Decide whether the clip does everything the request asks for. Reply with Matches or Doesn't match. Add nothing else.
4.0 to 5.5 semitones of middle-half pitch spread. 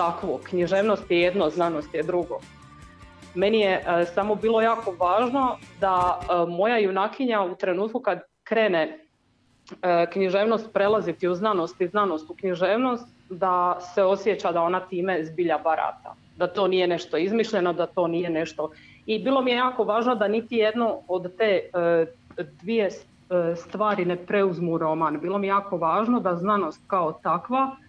Doesn't match